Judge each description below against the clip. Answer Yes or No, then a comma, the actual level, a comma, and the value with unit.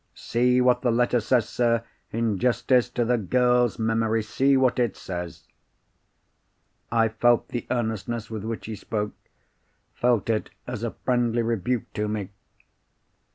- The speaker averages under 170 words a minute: Yes, average, 140 wpm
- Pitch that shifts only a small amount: Yes, narrow, 1.9 semitones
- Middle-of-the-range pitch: No, low, 115 Hz